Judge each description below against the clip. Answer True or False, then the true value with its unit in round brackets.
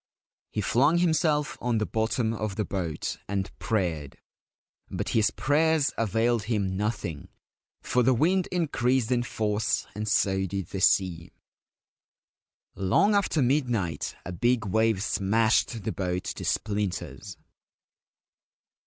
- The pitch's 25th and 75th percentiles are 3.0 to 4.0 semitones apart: False (4.5 semitones)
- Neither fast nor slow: False (125 wpm)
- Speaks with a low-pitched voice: True (110 Hz)